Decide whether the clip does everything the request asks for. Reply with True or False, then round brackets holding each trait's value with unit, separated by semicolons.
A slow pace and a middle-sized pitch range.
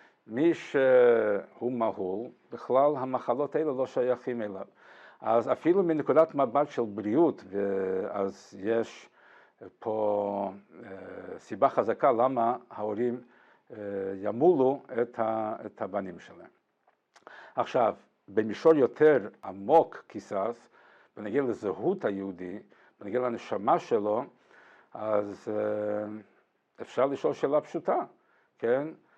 False (90 wpm; 6.1 semitones)